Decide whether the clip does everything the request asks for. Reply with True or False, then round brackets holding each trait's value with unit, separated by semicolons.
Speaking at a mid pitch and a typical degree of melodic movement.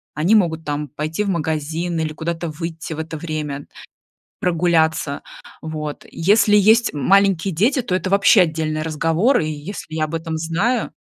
True (165 Hz; 3.3 semitones)